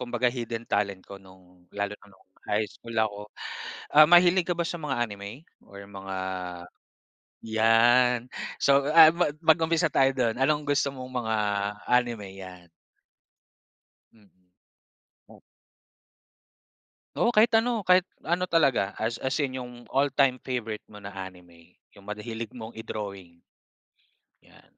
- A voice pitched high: No, low, 120 Hz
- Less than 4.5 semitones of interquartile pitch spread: No, wide, 5.4 semitones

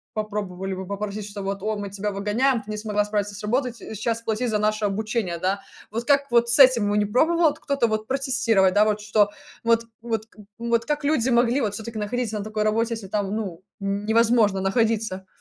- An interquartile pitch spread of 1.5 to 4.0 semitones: Yes, narrow, 2.4 semitones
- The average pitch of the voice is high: Yes, high, 215 Hz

